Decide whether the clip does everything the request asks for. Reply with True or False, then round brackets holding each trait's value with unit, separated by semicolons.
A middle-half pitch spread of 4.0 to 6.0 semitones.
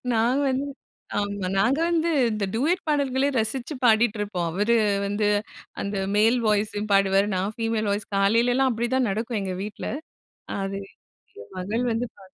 False (3.5 semitones)